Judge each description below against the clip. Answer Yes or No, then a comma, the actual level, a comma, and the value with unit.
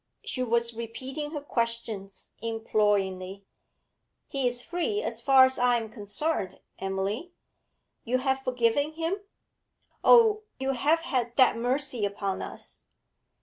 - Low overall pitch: No, high, 245 Hz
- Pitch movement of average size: Yes, average, 4.3 semitones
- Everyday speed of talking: No, slow, 125 wpm